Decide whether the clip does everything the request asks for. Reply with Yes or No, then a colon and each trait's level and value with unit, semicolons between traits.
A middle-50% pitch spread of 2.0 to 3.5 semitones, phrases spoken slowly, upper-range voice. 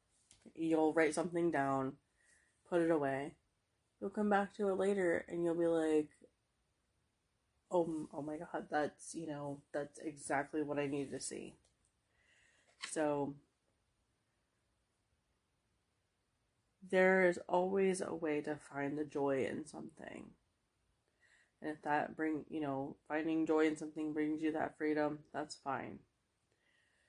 No: average, 2.8 semitones; slow, 130 wpm; medium, 150 Hz